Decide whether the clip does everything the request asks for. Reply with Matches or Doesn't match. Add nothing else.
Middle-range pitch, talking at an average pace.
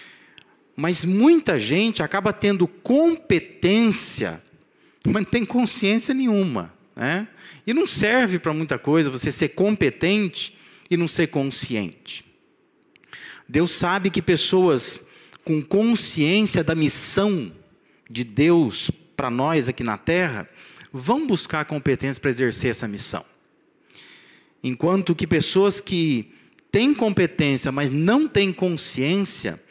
Doesn't match